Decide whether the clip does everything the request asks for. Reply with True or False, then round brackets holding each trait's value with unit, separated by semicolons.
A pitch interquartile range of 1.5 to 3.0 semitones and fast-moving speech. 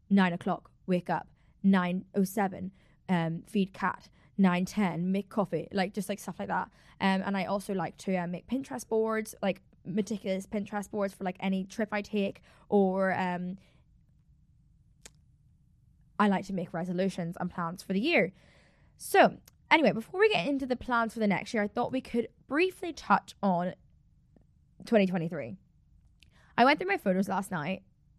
False (2.6 semitones; 170 wpm)